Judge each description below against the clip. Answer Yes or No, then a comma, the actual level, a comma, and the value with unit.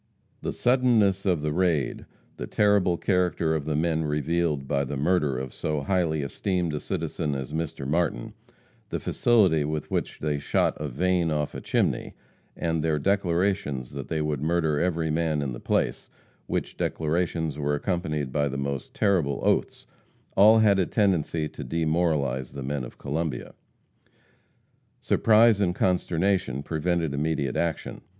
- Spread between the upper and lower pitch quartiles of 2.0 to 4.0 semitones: Yes, average, 3.7 semitones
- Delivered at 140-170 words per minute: Yes, average, 155 wpm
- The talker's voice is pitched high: No, very low, 80 Hz